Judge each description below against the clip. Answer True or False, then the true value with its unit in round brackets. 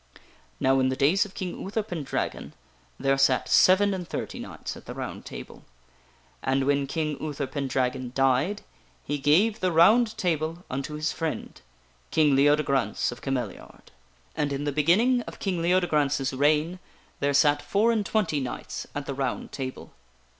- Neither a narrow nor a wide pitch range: True (4.8 semitones)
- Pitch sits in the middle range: True (145 Hz)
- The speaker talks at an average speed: True (170 wpm)